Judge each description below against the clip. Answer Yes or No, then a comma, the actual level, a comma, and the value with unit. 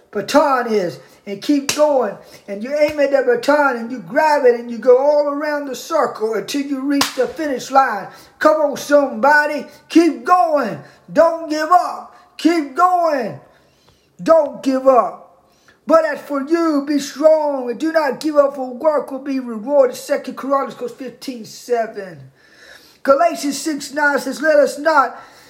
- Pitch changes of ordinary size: Yes, average, 3.1 semitones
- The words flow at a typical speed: Yes, average, 160 wpm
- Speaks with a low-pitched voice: No, very high, 280 Hz